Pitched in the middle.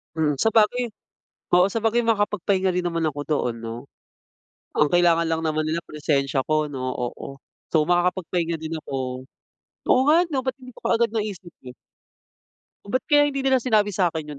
Yes: medium, 175 Hz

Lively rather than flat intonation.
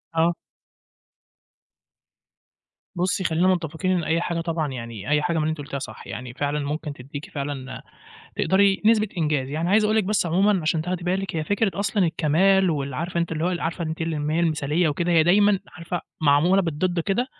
No: average, 3.6 semitones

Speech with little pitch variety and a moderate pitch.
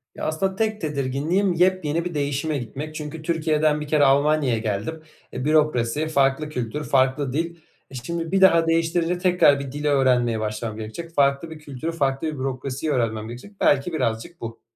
No: average, 3.9 semitones; medium, 150 Hz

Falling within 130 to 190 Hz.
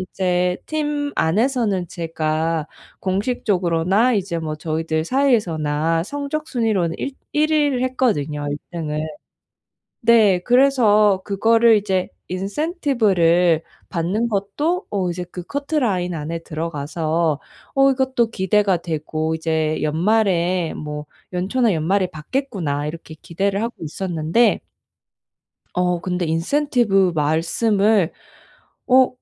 Yes: medium, 185 Hz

